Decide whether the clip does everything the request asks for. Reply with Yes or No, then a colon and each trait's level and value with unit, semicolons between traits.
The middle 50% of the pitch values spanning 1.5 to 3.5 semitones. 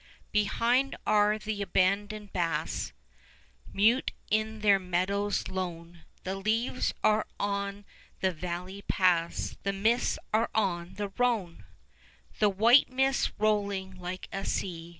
Yes: narrow, 2.6 semitones